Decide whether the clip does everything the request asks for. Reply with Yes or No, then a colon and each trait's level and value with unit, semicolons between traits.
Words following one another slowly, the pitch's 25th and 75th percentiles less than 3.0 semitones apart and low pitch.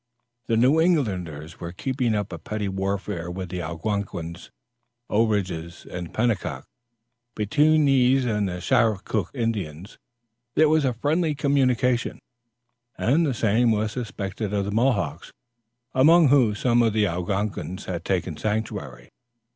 No: slow, 130 wpm; wide, 5.5 semitones; low, 105 Hz